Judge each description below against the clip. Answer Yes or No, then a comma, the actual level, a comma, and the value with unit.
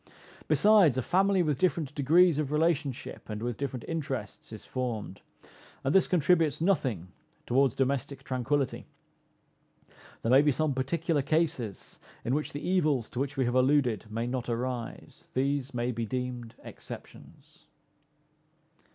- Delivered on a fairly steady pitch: No, average, 3.8 semitones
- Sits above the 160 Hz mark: No, low, 135 Hz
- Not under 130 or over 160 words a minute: Yes, average, 140 wpm